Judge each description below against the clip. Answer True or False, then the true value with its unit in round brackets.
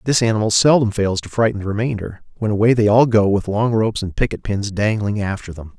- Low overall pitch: True (105 Hz)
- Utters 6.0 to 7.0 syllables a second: True (6.1 syllables/s)